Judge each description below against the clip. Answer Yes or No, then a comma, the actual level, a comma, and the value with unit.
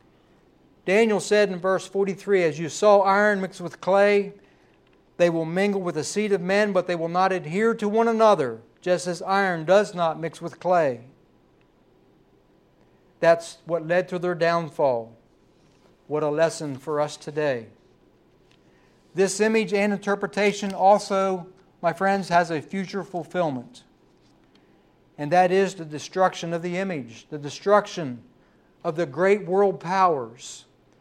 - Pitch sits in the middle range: Yes, medium, 180 Hz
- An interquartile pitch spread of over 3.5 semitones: No, average, 3.2 semitones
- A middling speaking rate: Yes, average, 145 wpm